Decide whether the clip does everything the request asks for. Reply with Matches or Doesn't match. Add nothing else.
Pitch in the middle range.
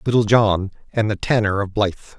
Doesn't match